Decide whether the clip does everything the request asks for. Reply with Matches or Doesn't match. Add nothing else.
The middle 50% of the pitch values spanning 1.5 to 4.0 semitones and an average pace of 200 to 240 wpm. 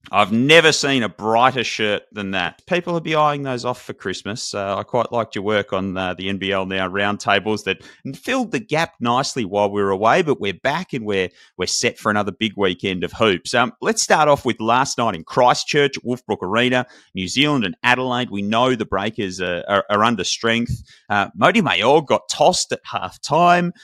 Doesn't match